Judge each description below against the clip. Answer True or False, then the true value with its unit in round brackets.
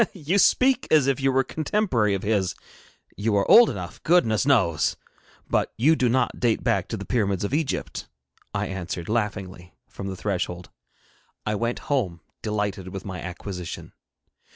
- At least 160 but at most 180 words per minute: True (165 wpm)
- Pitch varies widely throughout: True (6.0 semitones)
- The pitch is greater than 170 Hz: False (105 Hz)